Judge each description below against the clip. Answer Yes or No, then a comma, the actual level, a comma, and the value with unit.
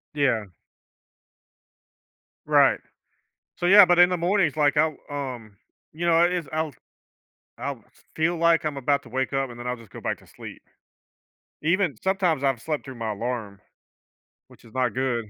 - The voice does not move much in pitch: No, average, 5.3 semitones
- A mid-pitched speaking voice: Yes, medium, 145 Hz